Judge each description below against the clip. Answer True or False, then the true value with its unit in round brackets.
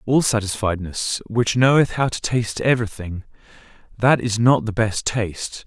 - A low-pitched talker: True (115 Hz)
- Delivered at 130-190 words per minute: True (140 wpm)